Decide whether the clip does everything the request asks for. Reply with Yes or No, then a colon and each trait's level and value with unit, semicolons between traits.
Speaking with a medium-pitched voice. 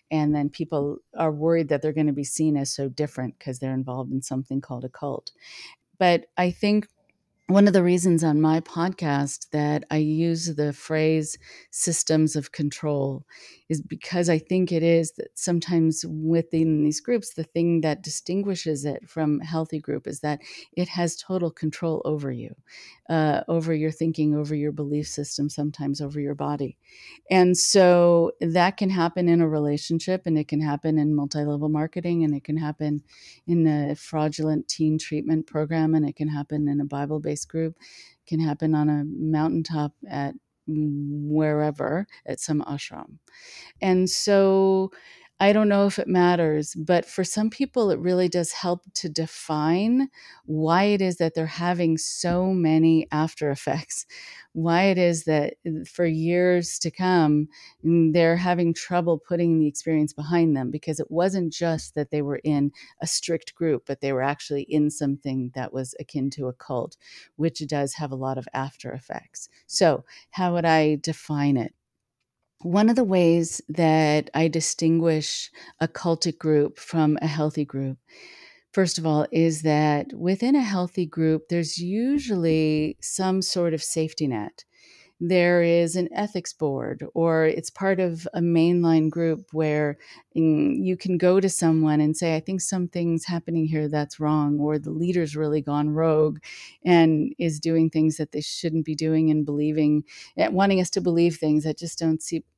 Yes: medium, 160 Hz